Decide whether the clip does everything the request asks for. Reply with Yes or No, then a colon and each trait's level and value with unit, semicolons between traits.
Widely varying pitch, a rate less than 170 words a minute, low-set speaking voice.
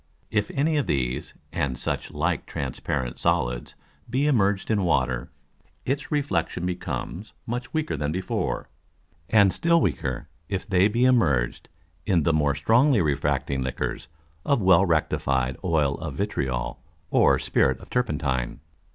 Yes: wide, 8.7 semitones; slow, 135 wpm; very low, 85 Hz